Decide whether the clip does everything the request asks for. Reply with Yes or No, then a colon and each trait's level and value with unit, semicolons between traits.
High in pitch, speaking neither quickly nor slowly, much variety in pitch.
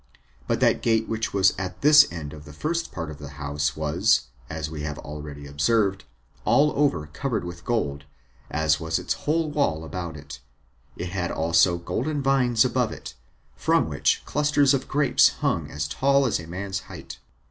No: very low, 90 Hz; average, 180 wpm; wide, 9.0 semitones